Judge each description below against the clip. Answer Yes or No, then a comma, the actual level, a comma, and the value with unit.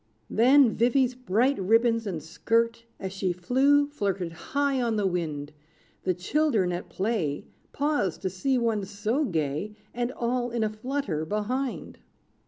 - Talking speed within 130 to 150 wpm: Yes, average, 145 wpm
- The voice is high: Yes, high, 225 Hz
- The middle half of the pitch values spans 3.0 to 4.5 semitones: No, wide, 5.4 semitones